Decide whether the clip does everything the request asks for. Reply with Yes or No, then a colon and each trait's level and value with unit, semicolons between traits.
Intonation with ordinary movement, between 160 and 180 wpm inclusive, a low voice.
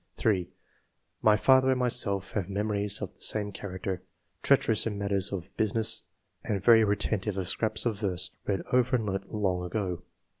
No: narrow, 2.3 semitones; average, 165 wpm; low, 100 Hz